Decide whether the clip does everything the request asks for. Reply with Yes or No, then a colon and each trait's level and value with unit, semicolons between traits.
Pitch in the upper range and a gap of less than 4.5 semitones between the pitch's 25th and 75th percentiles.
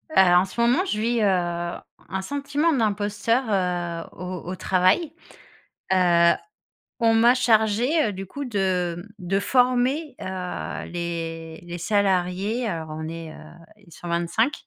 No: high, 195 Hz; average, 5.1 semitones